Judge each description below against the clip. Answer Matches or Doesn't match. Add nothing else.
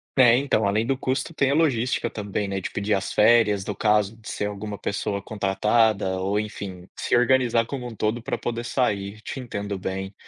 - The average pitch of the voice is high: Doesn't match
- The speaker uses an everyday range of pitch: Matches